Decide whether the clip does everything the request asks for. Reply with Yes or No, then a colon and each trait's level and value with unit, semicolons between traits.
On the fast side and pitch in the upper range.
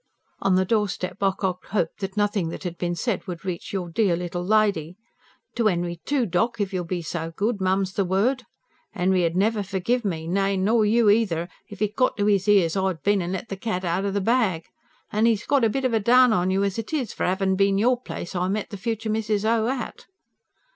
Yes: fast, 230 wpm; high, 195 Hz